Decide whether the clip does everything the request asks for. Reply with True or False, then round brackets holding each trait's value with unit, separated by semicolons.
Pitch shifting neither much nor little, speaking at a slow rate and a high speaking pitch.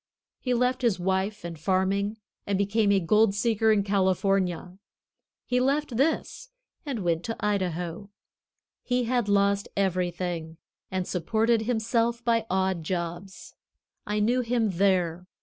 True (3.9 semitones; 130 wpm; 200 Hz)